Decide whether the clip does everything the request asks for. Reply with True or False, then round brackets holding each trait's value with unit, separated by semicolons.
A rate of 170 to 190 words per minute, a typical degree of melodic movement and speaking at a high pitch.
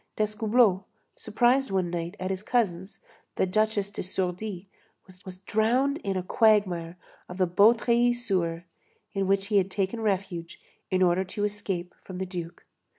False (150 wpm; 3.0 semitones; 195 Hz)